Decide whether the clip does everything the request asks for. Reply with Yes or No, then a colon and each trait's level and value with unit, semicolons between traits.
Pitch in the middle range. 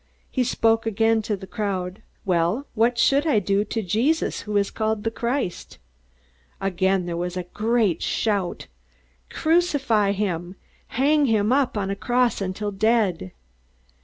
No: high, 210 Hz